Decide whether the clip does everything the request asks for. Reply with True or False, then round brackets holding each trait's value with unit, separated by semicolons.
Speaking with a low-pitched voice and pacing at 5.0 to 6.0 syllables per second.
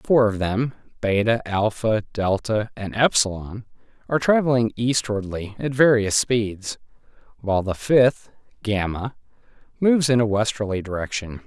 False (110 Hz; 4.5 syllables/s)